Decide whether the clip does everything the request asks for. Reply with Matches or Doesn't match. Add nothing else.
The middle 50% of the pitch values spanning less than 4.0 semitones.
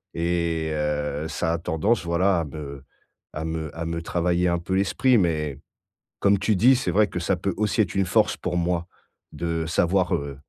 Matches